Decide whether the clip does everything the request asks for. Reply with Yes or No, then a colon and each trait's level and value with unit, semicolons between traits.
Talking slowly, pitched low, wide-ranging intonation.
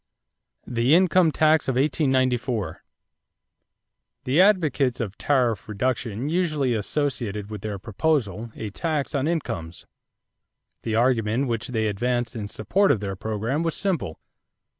Yes: slow, 125 wpm; low, 125 Hz; wide, 5.7 semitones